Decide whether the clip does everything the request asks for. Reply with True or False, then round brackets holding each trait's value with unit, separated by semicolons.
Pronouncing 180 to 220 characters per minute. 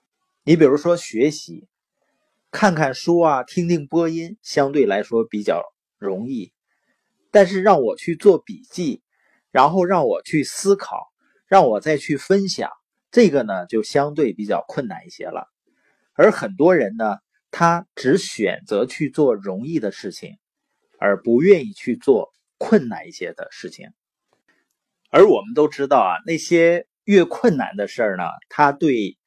True (210 characters per minute)